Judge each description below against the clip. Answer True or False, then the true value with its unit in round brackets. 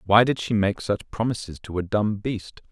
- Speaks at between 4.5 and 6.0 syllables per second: True (5.0 syllables/s)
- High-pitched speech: False (105 Hz)